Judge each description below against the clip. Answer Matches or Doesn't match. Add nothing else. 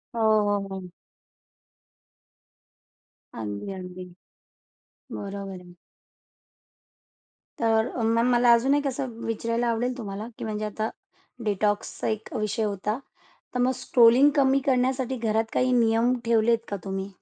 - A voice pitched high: Matches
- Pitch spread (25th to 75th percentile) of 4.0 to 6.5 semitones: Doesn't match